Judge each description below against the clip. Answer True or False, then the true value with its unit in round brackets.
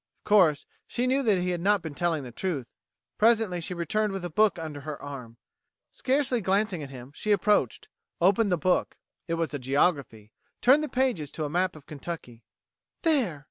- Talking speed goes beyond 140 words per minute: True (190 wpm)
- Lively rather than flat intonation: True (6.4 semitones)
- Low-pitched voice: False (175 Hz)